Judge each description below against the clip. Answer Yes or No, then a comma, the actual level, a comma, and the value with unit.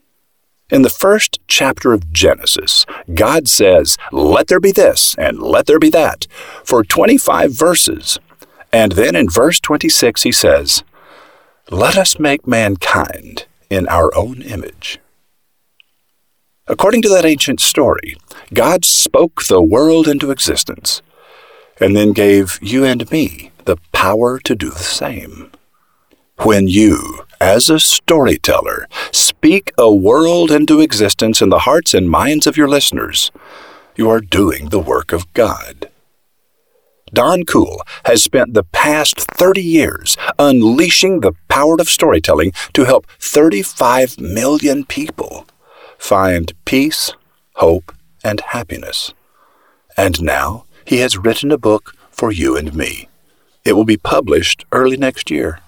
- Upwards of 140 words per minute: No, slow, 135 wpm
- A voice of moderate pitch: Yes, medium, 145 Hz